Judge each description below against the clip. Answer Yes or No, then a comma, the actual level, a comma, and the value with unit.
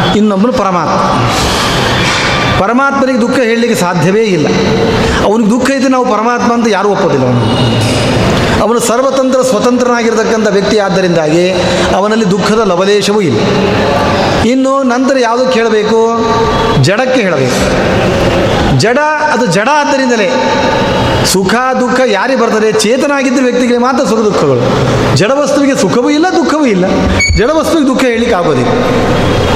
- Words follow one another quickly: Yes, fast, 110 wpm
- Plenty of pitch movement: No, average, 4.1 semitones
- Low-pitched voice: No, high, 235 Hz